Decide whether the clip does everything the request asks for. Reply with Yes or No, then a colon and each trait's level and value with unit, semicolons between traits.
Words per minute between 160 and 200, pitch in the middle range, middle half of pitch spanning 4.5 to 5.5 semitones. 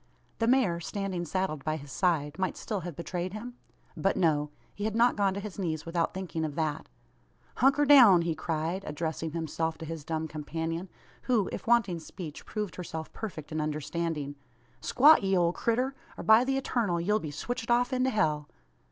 Yes: average, 185 wpm; medium, 175 Hz; average, 5.2 semitones